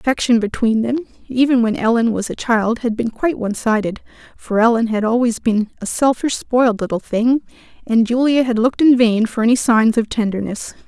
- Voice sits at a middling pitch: No, high, 230 Hz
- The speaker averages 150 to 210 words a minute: Yes, average, 195 wpm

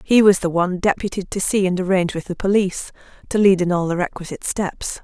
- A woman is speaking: Yes, female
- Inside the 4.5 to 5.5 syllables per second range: No, 6.4 syllables/s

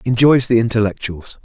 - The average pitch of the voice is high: No, low, 115 Hz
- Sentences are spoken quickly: No, slow, 125 wpm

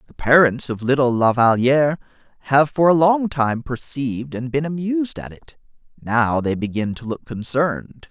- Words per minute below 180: Yes, average, 170 wpm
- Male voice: Yes, male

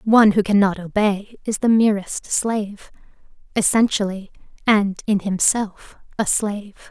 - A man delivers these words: No, female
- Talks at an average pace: No, slow, 120 wpm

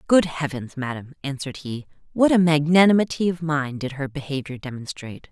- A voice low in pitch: No, medium, 150 Hz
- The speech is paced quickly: No, average, 160 wpm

